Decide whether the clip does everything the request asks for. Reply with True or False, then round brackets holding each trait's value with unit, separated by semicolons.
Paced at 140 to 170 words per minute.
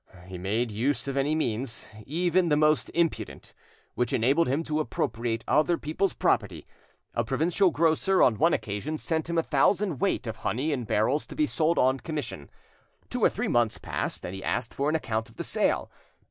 False (190 wpm)